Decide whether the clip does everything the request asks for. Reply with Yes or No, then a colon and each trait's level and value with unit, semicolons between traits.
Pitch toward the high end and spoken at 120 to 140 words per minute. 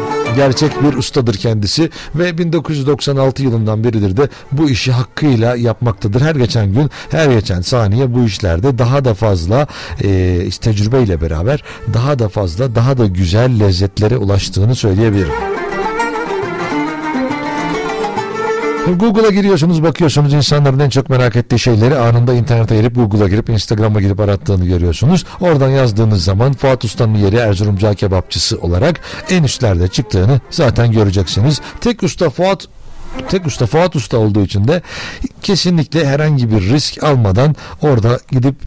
No: low, 125 Hz; average, 135 wpm